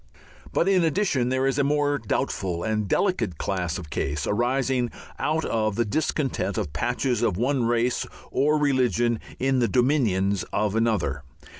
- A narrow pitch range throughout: No, average, 4.9 semitones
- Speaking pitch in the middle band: No, low, 120 Hz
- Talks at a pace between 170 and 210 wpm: No, average, 155 wpm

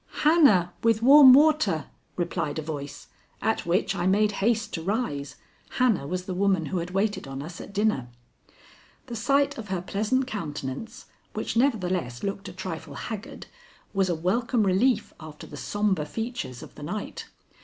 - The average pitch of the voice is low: No, high, 195 Hz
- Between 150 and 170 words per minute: Yes, average, 165 wpm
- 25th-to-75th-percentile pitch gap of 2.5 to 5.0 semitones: No, wide, 5.6 semitones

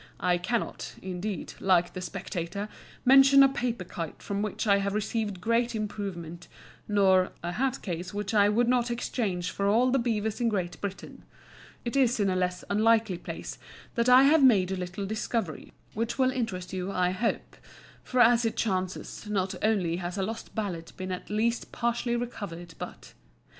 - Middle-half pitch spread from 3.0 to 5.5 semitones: Yes, average, 4.3 semitones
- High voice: Yes, high, 205 Hz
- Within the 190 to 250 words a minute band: No, average, 175 wpm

